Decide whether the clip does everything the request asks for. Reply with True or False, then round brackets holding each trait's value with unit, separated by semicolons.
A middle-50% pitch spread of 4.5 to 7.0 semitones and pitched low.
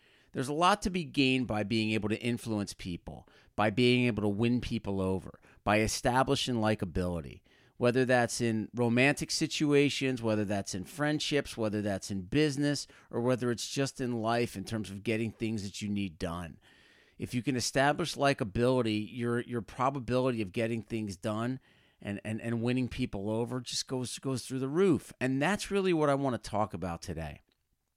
False (4.0 semitones; 120 Hz)